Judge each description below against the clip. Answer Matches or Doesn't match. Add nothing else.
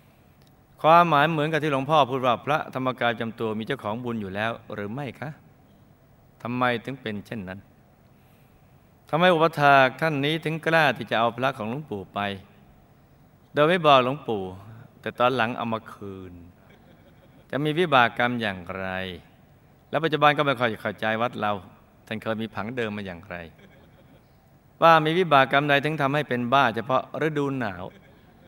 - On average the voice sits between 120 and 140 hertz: Matches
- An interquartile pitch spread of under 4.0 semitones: Doesn't match